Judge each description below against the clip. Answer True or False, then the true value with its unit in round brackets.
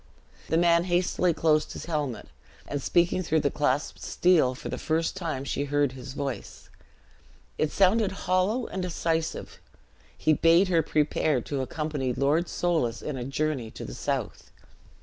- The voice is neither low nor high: True (155 Hz)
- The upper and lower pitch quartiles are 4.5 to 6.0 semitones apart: False (3.7 semitones)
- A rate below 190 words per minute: True (155 wpm)